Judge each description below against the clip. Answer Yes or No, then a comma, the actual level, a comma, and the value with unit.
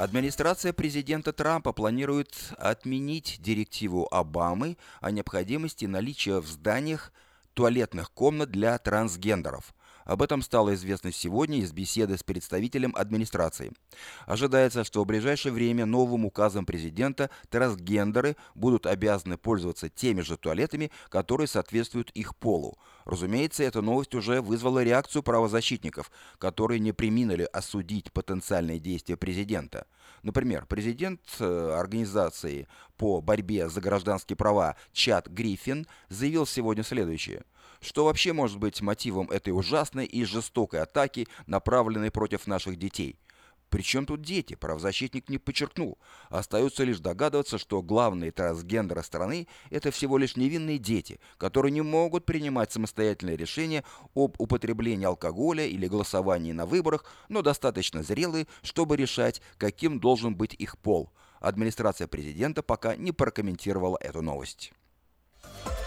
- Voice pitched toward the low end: Yes, low, 110 Hz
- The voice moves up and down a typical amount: No, wide, 5.7 semitones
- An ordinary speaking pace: Yes, average, 120 wpm